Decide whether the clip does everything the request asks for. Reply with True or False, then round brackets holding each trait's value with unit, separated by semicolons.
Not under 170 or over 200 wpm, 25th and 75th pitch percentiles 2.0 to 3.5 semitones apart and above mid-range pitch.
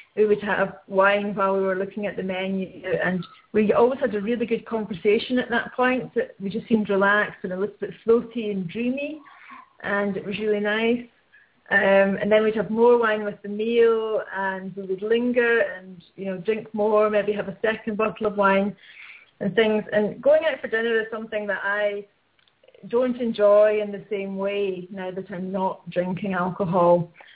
True (190 wpm; 2.6 semitones; 210 Hz)